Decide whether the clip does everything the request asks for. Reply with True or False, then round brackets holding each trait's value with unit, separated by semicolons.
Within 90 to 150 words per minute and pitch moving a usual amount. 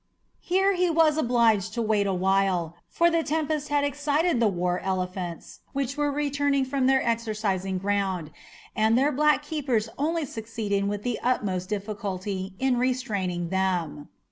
False (145 wpm; 6.9 semitones)